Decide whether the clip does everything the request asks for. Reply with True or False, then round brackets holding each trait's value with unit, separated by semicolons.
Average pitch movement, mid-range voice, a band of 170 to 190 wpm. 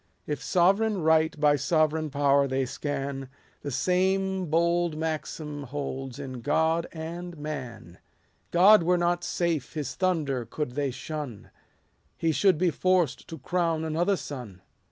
False (3.7 semitones; 155 Hz; 135 wpm)